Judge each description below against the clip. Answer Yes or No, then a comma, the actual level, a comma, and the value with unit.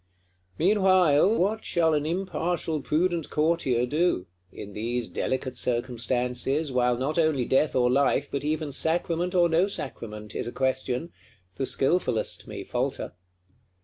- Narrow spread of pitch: No, average, 5.3 semitones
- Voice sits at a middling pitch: Yes, medium, 150 Hz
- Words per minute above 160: No, slow, 135 wpm